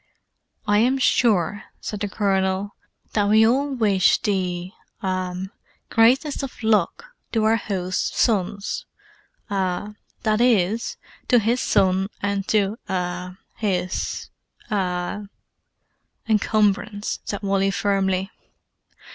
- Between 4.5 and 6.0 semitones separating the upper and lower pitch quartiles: No, average, 2.7 semitones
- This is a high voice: Yes, high, 205 Hz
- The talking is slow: Yes, slow, 90 wpm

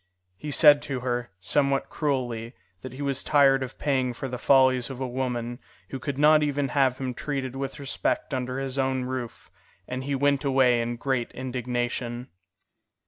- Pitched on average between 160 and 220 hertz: No, low, 130 Hz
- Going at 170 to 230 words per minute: Yes, average, 175 wpm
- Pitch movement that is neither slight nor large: No, narrow, 1.8 semitones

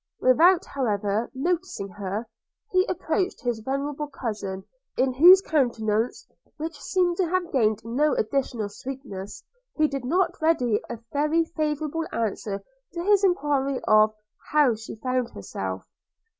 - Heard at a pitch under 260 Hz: No, very high, 270 Hz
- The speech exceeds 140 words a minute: No, slow, 135 wpm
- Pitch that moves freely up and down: Yes, wide, 6.8 semitones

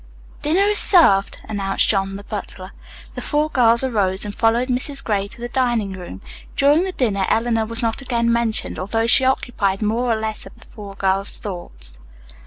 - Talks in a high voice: Yes, high, 225 Hz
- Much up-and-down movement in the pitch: No, average, 4.0 semitones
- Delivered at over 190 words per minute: No, average, 185 wpm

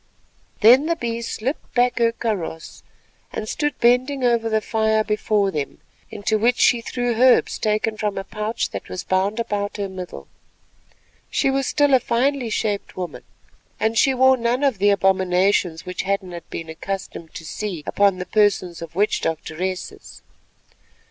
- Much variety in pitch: No, average, 4.1 semitones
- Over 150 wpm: Yes, average, 160 wpm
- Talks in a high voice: Yes, high, 215 Hz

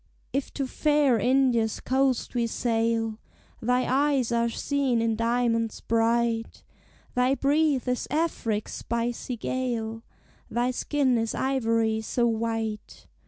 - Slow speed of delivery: Yes, slow, 120 wpm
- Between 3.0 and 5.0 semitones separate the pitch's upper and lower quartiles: No, narrow, 2.5 semitones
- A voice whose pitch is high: Yes, high, 235 Hz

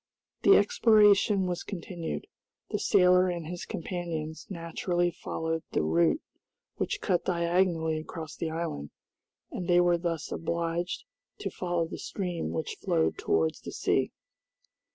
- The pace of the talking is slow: Yes, slow, 130 wpm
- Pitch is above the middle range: No, medium, 170 Hz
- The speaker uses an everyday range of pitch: No, narrow, 1.9 semitones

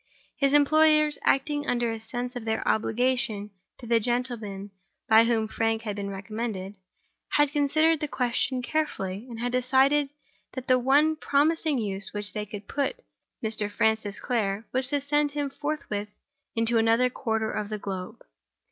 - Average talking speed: Yes, average, 160 wpm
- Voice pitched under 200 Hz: No, high, 240 Hz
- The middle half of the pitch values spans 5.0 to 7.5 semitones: No, average, 4.6 semitones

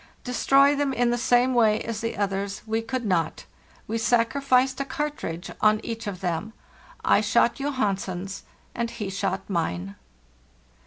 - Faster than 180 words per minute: No, average, 155 wpm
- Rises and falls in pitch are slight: No, average, 4.5 semitones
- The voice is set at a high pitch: Yes, high, 225 Hz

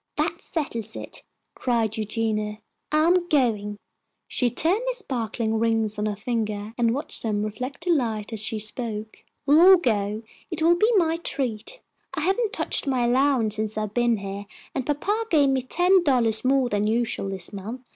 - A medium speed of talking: Yes, average, 175 wpm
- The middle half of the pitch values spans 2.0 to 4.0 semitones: No, wide, 5.5 semitones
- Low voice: No, high, 235 Hz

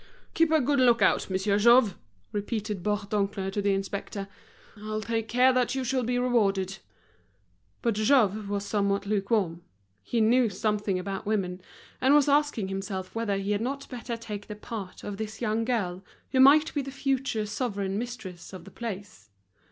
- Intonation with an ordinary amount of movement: Yes, average, 3.7 semitones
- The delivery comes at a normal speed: Yes, average, 170 wpm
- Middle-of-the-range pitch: No, high, 215 Hz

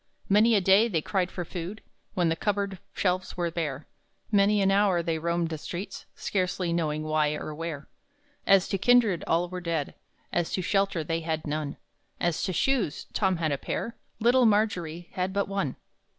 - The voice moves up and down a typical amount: Yes, average, 3.4 semitones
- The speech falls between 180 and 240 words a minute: Yes, average, 185 wpm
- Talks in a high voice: No, medium, 180 Hz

